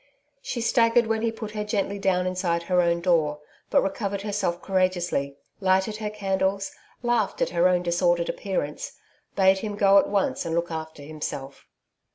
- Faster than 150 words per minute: Yes, average, 170 wpm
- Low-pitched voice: No, high, 190 Hz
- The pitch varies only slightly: No, average, 3.2 semitones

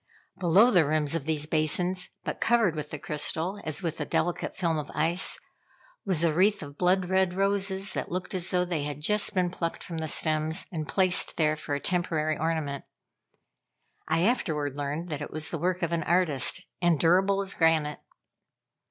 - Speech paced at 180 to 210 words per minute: Yes, average, 185 wpm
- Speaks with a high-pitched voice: No, medium, 165 Hz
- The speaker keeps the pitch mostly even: No, average, 3.1 semitones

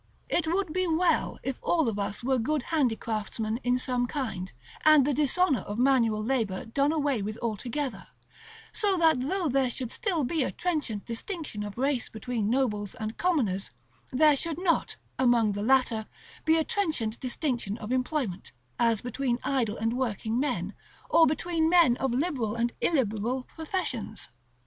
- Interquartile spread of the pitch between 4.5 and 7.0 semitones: Yes, wide, 5.5 semitones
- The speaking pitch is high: Yes, very high, 255 Hz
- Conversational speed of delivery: Yes, average, 160 wpm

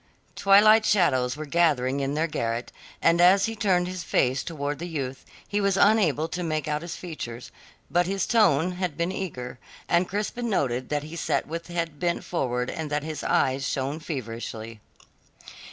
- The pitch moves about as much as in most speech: Yes, average, 5.0 semitones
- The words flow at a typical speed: Yes, average, 175 wpm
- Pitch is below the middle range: No, medium, 160 Hz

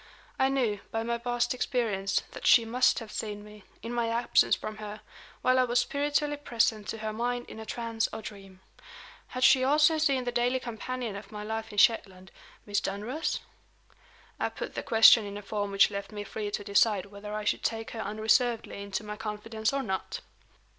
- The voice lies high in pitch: Yes, high, 220 Hz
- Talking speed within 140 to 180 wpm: No, average, 195 wpm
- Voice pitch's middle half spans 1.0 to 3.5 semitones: Yes, average, 2.8 semitones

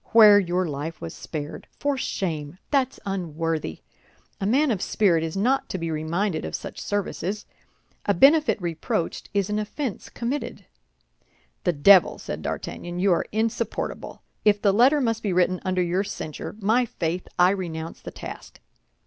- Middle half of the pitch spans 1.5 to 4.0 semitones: No, average, 4.5 semitones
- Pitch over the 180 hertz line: Yes, high, 190 Hz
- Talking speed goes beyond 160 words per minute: No, average, 155 wpm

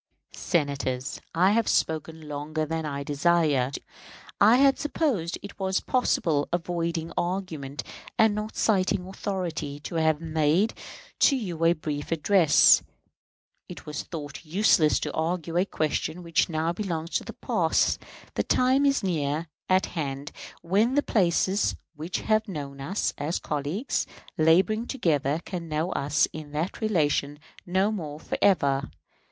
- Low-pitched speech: No, medium, 165 Hz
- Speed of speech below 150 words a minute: Yes, average, 140 wpm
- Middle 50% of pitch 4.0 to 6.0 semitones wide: Yes, average, 4.3 semitones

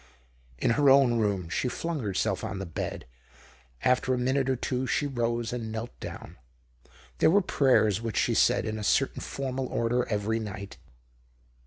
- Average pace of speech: Yes, average, 170 wpm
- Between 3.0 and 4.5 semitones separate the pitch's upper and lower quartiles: Yes, average, 3.3 semitones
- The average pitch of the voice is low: Yes, low, 120 Hz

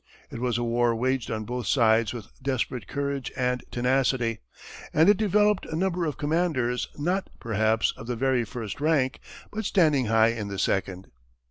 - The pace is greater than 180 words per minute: No, average, 170 wpm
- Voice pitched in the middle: No, low, 125 Hz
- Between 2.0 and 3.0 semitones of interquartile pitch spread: No, average, 4.4 semitones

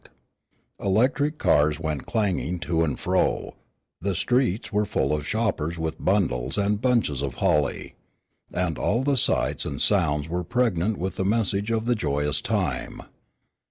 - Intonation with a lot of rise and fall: Yes, wide, 6.3 semitones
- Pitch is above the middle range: No, very low, 95 Hz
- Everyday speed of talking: Yes, average, 155 wpm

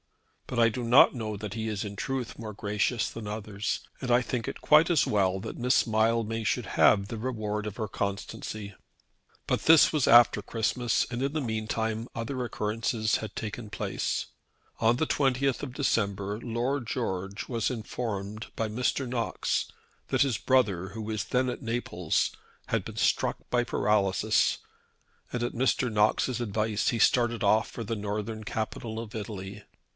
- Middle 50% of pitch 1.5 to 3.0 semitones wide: Yes, narrow, 2.6 semitones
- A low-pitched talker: Yes, low, 110 Hz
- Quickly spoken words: No, average, 170 wpm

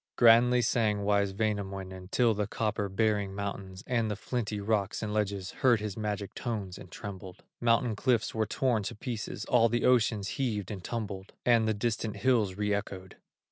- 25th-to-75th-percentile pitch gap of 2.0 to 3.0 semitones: Yes, narrow, 2.5 semitones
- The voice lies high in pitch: No, low, 105 Hz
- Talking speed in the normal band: Yes, average, 175 wpm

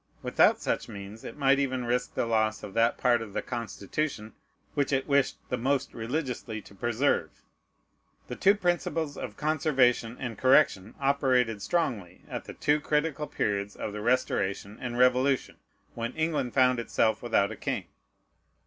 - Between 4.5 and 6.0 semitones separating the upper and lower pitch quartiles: No, average, 4.1 semitones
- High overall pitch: No, low, 125 Hz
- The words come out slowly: No, average, 155 wpm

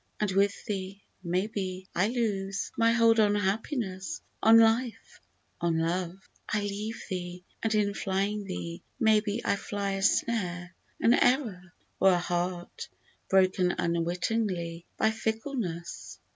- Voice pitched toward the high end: Yes, high, 195 Hz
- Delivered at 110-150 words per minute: Yes, slow, 135 wpm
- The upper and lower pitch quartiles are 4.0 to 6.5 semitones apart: No, average, 3.4 semitones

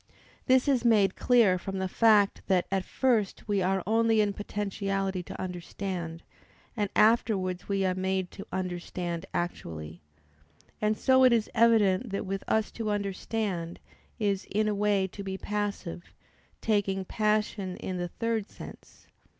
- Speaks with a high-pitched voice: Yes, high, 200 Hz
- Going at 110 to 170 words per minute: Yes, average, 150 wpm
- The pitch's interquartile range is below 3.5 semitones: Yes, narrow, 2.5 semitones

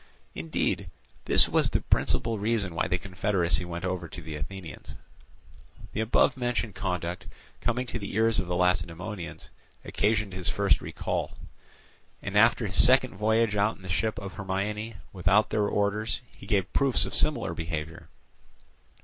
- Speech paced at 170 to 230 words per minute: No, average, 155 wpm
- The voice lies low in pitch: Yes, low, 100 Hz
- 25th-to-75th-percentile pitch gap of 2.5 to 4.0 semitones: Yes, average, 3.5 semitones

